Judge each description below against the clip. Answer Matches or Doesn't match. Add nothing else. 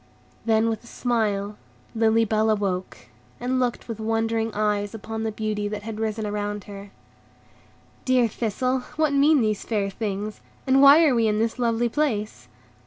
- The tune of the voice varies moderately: Doesn't match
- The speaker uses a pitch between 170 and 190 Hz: Doesn't match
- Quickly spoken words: Doesn't match